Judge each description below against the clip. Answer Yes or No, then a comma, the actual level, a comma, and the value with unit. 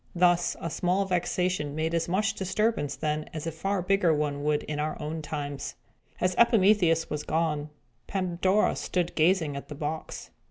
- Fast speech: No, average, 165 wpm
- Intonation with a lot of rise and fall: No, average, 3.5 semitones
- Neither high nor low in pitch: Yes, medium, 165 Hz